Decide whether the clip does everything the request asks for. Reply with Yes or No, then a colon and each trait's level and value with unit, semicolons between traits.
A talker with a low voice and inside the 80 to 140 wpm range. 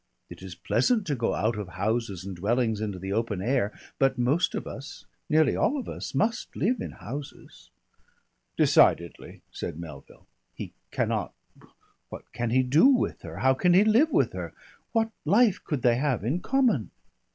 No: low, 130 Hz; average, 175 wpm